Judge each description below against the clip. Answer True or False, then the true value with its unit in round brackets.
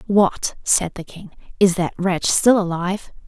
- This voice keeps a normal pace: True (165 wpm)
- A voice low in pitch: False (185 Hz)